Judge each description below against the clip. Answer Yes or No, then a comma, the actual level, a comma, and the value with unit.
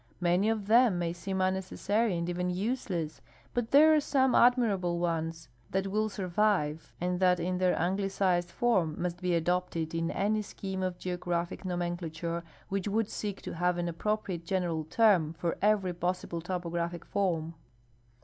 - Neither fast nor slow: Yes, average, 160 wpm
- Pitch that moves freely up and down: No, average, 2.8 semitones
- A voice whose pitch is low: No, medium, 180 Hz